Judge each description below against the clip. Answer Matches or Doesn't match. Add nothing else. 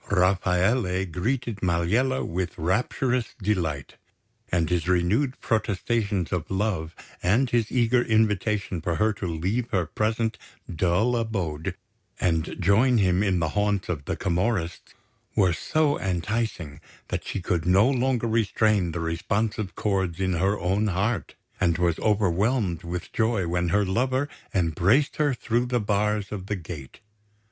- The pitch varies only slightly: Doesn't match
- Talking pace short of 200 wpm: Matches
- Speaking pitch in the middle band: Doesn't match